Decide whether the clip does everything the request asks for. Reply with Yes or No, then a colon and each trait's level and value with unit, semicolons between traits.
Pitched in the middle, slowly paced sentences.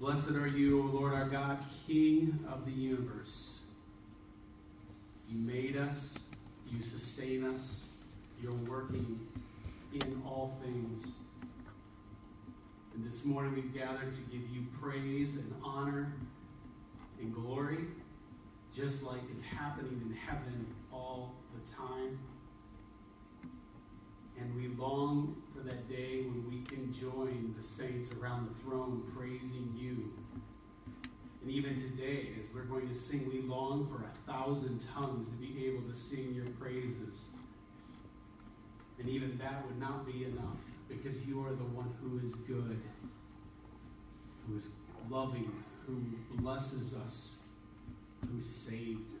No: low, 125 Hz; slow, 130 wpm